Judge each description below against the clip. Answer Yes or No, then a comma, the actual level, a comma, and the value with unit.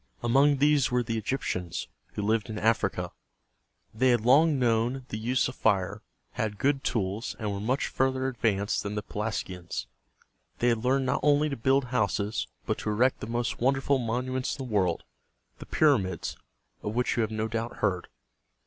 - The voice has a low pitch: Yes, low, 115 Hz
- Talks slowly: No, average, 185 wpm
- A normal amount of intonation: Yes, average, 3.7 semitones